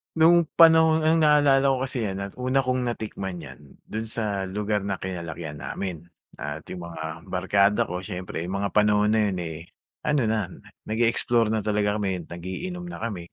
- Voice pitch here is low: Yes, low, 105 Hz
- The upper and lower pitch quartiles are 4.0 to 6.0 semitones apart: Yes, wide, 5.5 semitones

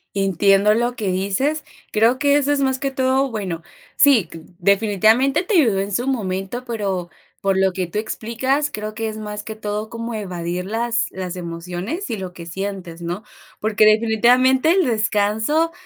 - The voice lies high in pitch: Yes, high, 215 Hz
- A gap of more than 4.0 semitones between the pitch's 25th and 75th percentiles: Yes, average, 4.7 semitones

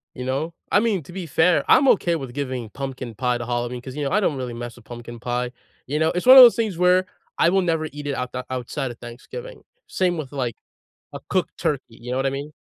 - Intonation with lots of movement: Yes, wide, 5.9 semitones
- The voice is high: No, low, 135 Hz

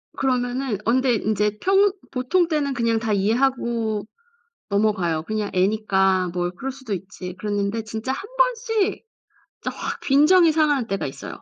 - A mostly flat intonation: No, average, 5.2 semitones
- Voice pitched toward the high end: Yes, high, 230 Hz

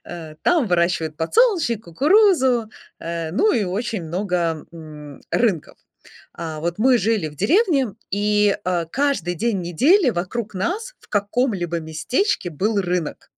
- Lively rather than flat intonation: Yes, wide, 6.5 semitones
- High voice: Yes, high, 200 Hz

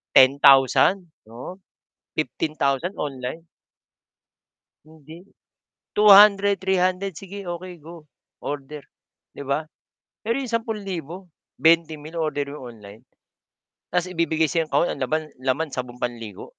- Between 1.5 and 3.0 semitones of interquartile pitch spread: No, average, 4.8 semitones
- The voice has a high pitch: No, medium, 160 Hz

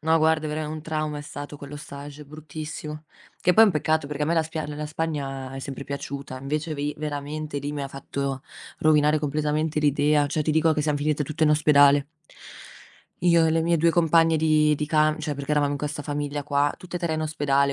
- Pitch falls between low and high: Yes, medium, 150 Hz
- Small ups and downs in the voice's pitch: Yes, narrow, 1.5 semitones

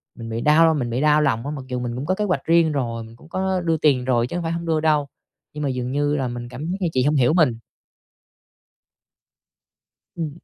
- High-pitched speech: No, medium, 145 Hz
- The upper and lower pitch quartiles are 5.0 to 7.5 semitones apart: No, average, 4.6 semitones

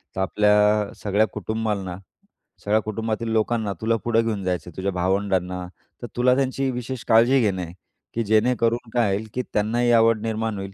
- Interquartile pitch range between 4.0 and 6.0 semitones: No, average, 2.8 semitones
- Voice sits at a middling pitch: No, low, 110 Hz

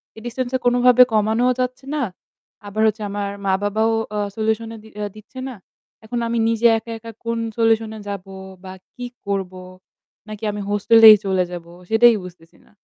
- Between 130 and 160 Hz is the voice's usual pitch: No, high, 220 Hz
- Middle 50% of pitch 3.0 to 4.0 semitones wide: No, narrow, 2.4 semitones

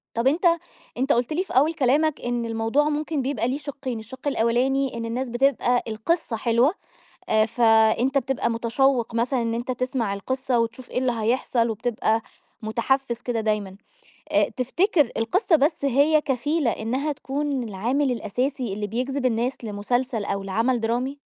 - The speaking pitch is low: No, very high, 250 Hz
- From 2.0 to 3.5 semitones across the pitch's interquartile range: Yes, average, 3.2 semitones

